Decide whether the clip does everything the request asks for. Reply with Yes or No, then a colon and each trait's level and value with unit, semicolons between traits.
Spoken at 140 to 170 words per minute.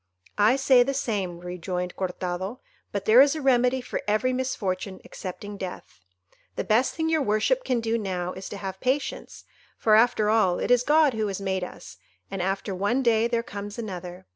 No: average, 190 wpm